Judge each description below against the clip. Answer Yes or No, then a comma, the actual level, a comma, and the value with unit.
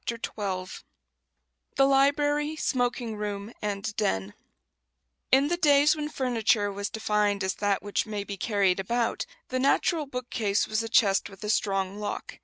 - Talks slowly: No, average, 155 wpm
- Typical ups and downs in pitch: Yes, average, 4.7 semitones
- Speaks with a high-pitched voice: Yes, high, 215 Hz